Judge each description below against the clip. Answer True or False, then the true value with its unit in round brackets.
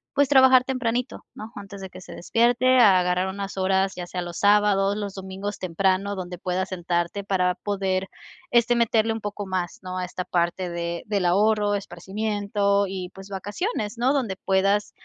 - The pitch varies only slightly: True (2.3 semitones)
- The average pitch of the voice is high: True (195 Hz)